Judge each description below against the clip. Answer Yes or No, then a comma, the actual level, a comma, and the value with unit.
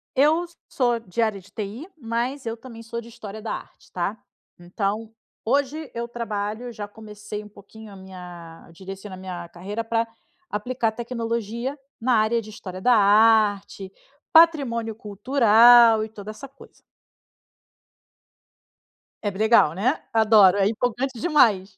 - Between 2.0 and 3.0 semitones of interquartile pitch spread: Yes, average, 2.7 semitones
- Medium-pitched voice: No, high, 220 Hz